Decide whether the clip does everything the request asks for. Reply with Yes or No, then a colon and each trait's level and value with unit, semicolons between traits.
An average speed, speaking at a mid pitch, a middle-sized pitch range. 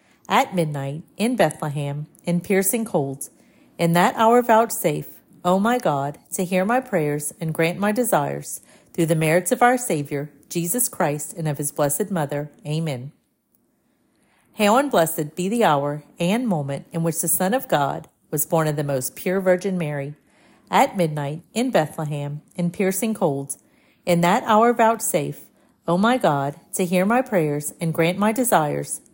No: average, 170 wpm; medium, 175 Hz; wide, 6.2 semitones